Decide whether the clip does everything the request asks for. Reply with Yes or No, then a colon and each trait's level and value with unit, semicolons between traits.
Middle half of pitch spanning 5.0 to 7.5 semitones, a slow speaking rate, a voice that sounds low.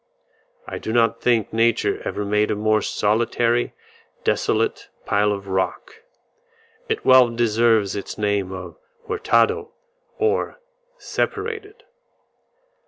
No: average, 3.9 semitones; slow, 105 wpm; low, 115 Hz